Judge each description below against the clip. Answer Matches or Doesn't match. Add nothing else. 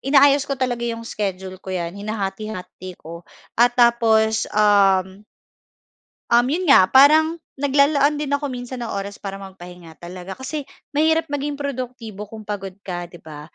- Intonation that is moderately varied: Doesn't match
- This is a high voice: Matches